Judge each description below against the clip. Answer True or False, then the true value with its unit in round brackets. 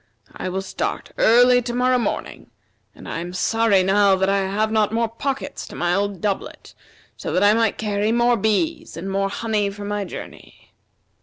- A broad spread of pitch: False (2.9 semitones)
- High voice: True (210 Hz)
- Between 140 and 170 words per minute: False (185 wpm)